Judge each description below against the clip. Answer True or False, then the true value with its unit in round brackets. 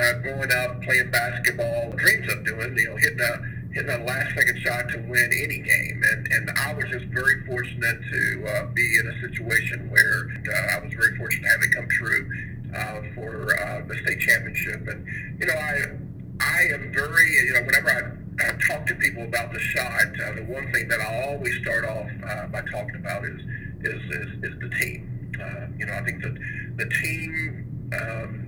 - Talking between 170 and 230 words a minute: True (195 wpm)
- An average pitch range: False (1.5 semitones)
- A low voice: True (120 Hz)